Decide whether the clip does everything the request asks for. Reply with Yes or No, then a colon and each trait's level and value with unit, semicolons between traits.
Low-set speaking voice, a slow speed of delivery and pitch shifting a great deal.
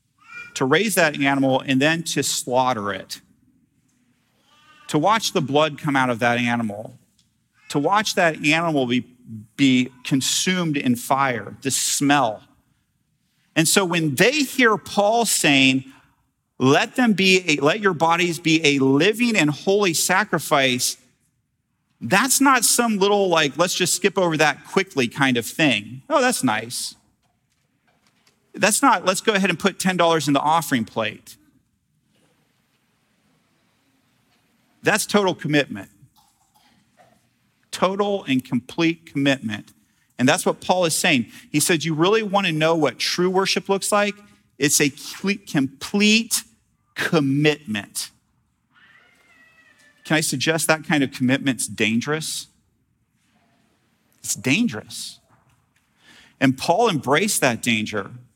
No: medium, 155 Hz; slow, 125 wpm; wide, 6.5 semitones